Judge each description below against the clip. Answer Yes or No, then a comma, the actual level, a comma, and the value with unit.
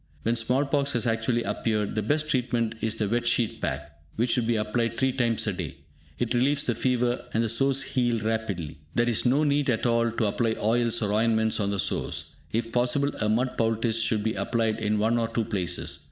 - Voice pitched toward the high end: No, low, 115 Hz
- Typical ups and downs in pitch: No, narrow, 1.9 semitones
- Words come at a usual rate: No, fast, 215 wpm